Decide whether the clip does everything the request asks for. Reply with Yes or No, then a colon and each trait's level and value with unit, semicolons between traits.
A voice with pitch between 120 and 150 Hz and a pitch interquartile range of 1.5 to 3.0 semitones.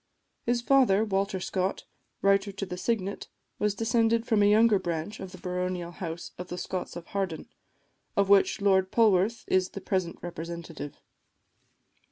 No: high, 195 Hz; narrow, 2.6 semitones